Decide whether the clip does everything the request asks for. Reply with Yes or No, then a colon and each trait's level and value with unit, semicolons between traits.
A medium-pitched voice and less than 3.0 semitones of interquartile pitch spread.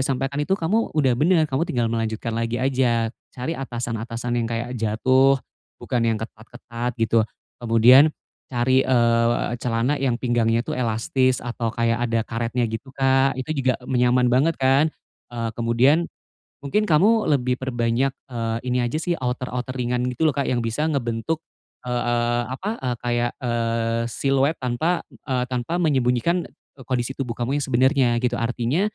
No: low, 125 Hz; narrow, 2.5 semitones